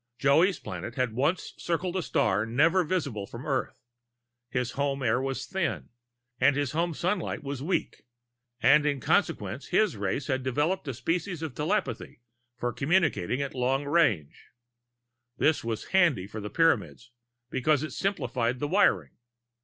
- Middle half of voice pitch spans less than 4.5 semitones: No, average, 5.2 semitones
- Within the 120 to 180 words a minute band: Yes, average, 150 wpm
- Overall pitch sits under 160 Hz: Yes, medium, 140 Hz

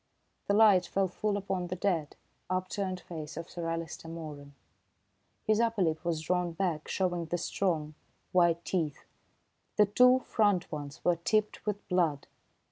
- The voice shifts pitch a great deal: No, average, 3.4 semitones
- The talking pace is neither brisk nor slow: Yes, average, 150 wpm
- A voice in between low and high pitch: Yes, medium, 180 Hz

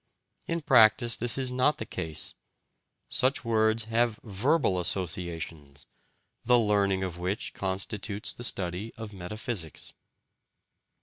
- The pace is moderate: No, slow, 115 wpm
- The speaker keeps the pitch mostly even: No, average, 4.4 semitones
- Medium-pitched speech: No, low, 105 Hz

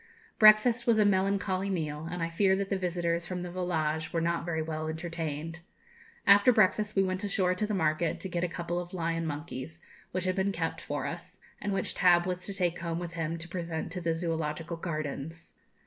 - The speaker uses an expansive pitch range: No, narrow, 2.5 semitones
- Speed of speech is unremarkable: No, fast, 210 wpm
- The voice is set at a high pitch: No, medium, 175 Hz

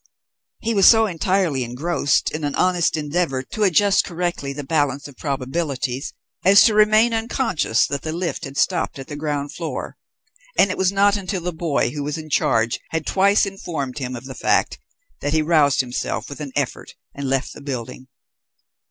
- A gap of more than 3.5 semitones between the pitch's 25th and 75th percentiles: Yes, average, 5.1 semitones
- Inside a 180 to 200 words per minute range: Yes, average, 185 wpm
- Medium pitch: Yes, medium, 155 Hz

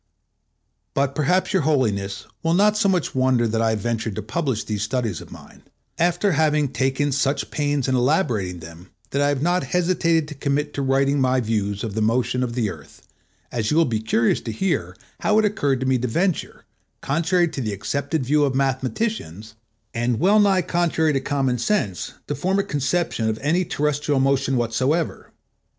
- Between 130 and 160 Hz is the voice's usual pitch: Yes, low, 135 Hz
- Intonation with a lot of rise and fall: Yes, wide, 5.8 semitones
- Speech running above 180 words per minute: Yes, average, 190 wpm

